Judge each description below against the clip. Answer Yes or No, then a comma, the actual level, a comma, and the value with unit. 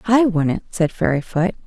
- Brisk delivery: No, average, 145 wpm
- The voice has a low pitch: No, medium, 185 Hz